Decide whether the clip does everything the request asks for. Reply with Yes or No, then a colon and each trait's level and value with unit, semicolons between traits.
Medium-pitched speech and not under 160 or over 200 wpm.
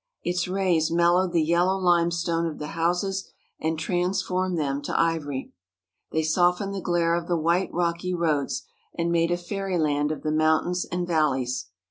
Yes: medium, 170 Hz; average, 165 wpm